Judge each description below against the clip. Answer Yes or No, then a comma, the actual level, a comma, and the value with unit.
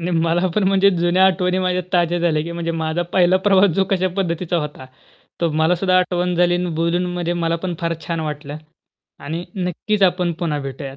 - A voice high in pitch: No, medium, 175 Hz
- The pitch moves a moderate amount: No, narrow, 1.7 semitones